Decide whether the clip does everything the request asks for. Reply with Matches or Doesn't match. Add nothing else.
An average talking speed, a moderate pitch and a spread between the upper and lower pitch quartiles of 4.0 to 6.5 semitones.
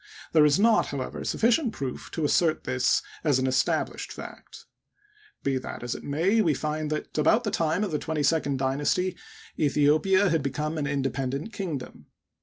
Matches